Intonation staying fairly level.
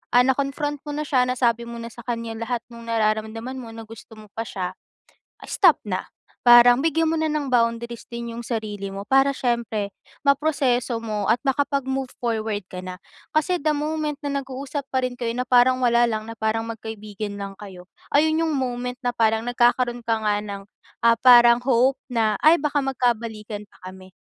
No: average, 3.4 semitones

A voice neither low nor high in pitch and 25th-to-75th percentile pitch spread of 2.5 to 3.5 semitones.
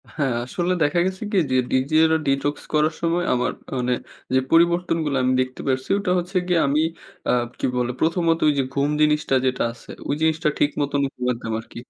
No: medium, 145 Hz; average, 4.2 semitones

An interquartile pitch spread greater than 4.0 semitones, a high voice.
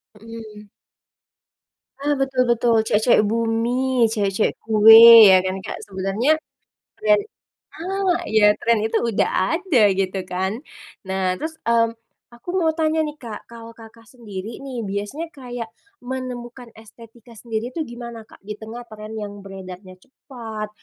No: average, 3.0 semitones; high, 230 Hz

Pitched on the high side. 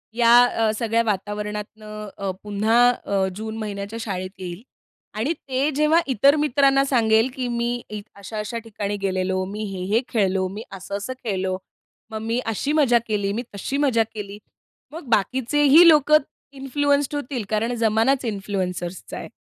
Yes: high, 220 Hz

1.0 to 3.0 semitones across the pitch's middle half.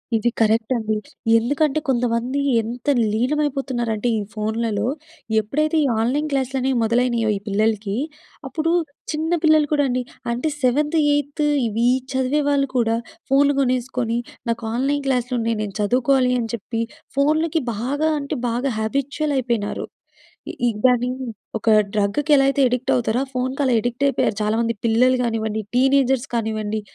No: average, 3.5 semitones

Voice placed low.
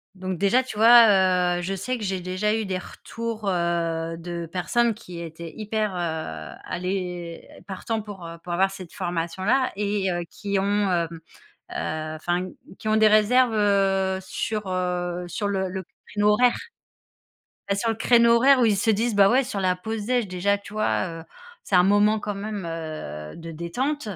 No: high, 195 Hz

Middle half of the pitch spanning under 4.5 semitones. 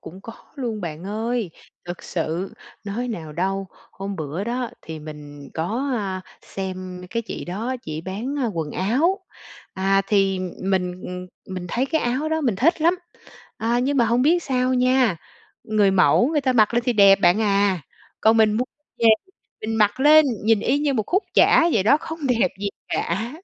No: average, 5.2 semitones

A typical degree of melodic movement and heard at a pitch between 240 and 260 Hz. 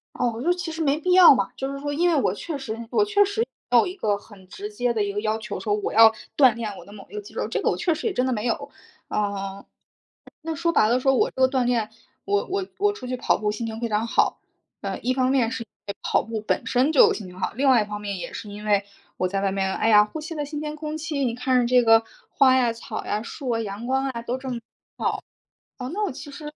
No: wide, 5.8 semitones; high, 245 Hz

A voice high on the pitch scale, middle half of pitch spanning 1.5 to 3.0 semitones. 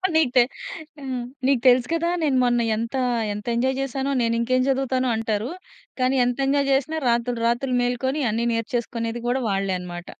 Yes: high, 245 Hz; narrow, 2.4 semitones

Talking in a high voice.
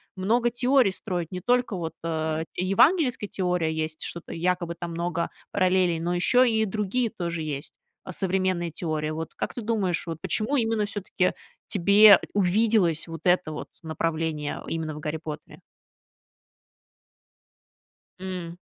No: medium, 180 Hz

